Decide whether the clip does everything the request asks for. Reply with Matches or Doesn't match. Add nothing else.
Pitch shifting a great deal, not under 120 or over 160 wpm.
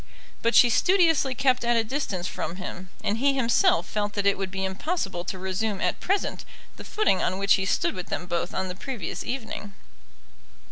Doesn't match